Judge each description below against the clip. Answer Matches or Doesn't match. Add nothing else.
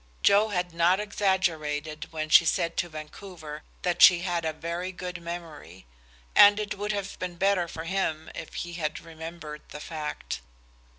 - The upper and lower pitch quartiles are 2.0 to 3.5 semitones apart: Matches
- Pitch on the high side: Doesn't match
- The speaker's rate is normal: Matches